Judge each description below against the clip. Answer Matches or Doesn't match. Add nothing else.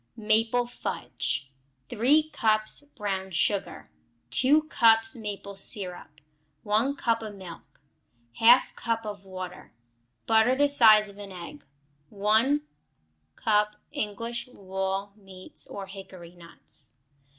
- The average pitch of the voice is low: Doesn't match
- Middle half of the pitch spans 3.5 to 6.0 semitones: Doesn't match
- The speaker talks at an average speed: Doesn't match